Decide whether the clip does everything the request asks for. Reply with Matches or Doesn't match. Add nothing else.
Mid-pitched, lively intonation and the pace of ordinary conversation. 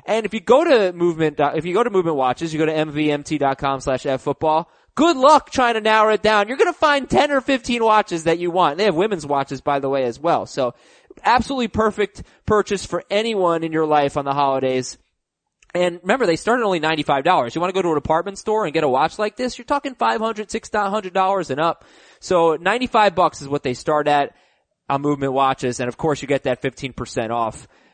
Doesn't match